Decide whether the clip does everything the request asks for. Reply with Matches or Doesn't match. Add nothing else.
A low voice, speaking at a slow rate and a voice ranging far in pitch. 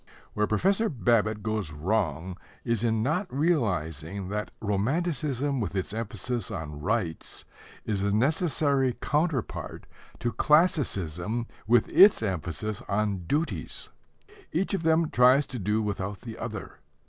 Matches